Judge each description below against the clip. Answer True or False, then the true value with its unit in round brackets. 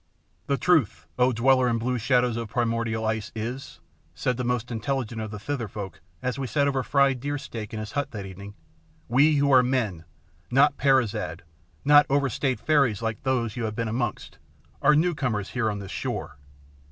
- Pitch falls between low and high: False (120 Hz)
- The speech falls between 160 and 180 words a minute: False (190 wpm)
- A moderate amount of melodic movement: True (3.7 semitones)